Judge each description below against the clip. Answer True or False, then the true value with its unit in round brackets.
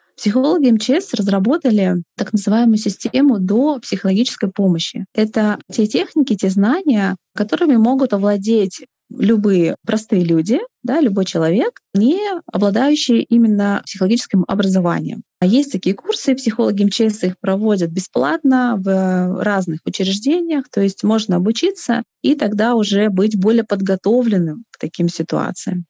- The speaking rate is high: False (125 wpm)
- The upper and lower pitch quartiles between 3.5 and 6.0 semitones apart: True (4.3 semitones)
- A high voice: True (215 Hz)